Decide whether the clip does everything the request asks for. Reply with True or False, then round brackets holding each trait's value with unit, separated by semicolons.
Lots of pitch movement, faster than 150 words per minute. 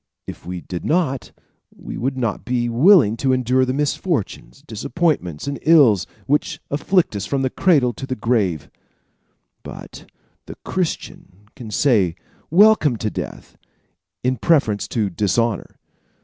False (5.7 semitones; 135 wpm)